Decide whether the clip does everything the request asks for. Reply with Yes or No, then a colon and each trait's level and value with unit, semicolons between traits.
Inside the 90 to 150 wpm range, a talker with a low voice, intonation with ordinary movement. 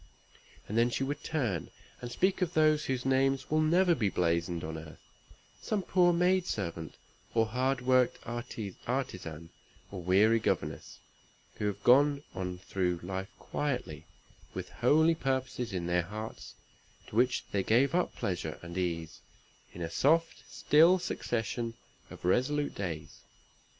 No: average, 145 wpm; low, 120 Hz; wide, 8.0 semitones